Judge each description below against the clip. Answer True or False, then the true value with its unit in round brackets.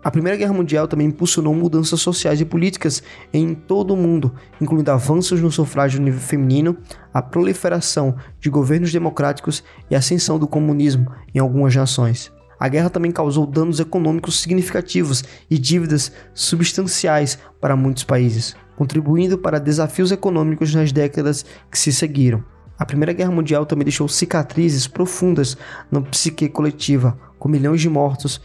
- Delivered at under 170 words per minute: True (150 wpm)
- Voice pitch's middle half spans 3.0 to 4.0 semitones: True (3.3 semitones)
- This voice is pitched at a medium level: True (155 Hz)